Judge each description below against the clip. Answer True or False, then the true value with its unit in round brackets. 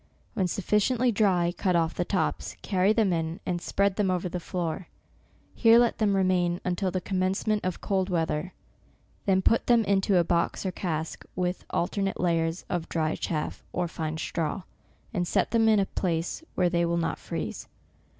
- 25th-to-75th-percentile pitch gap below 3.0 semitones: True (2.5 semitones)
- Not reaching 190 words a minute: True (180 wpm)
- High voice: False (180 Hz)